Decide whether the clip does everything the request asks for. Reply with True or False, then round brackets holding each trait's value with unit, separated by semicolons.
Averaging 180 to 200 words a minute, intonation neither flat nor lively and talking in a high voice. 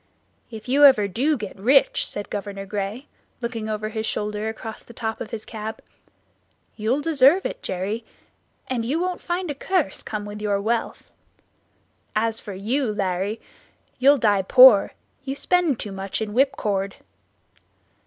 False (155 wpm; 4.4 semitones; 220 Hz)